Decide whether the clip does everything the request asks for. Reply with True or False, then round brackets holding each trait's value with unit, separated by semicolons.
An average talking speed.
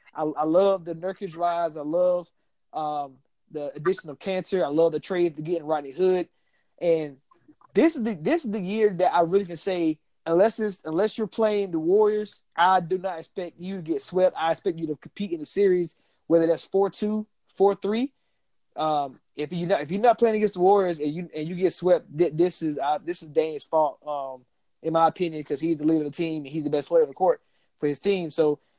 False (230 wpm)